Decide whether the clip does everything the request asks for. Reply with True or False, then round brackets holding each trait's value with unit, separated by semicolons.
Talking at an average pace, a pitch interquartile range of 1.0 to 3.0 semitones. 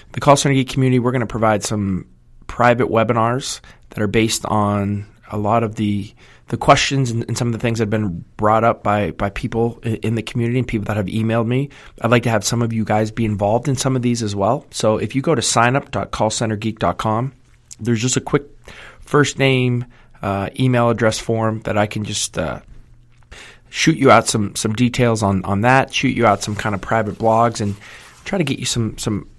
False (215 wpm; 2.5 semitones)